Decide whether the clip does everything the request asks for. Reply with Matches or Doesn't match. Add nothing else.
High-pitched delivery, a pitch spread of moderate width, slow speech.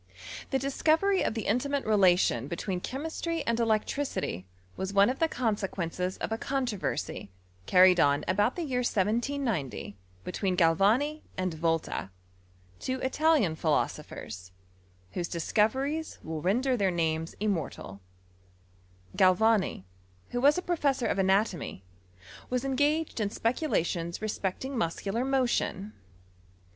Doesn't match